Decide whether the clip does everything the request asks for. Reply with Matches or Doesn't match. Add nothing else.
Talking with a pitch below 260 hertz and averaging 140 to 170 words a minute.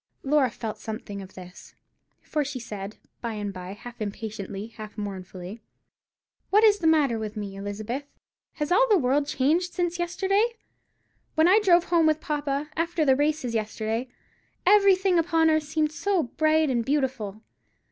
Doesn't match